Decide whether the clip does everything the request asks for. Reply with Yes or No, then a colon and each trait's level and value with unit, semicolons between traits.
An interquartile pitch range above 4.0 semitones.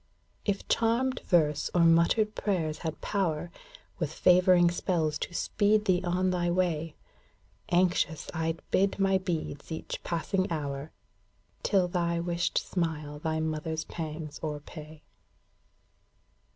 No: average, 2.7 semitones